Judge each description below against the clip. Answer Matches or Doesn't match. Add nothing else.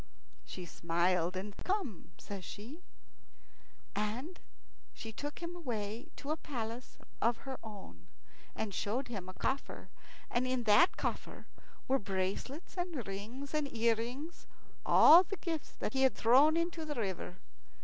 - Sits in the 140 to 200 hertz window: Doesn't match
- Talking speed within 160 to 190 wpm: Doesn't match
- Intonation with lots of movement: Matches